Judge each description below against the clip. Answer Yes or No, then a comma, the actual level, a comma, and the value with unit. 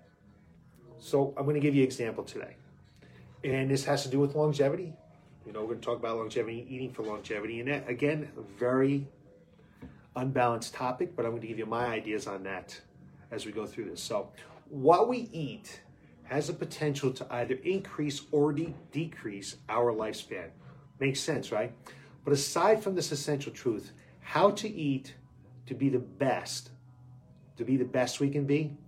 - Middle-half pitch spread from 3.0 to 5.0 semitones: Yes, average, 3.5 semitones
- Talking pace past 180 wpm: No, average, 175 wpm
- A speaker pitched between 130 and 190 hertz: Yes, low, 135 Hz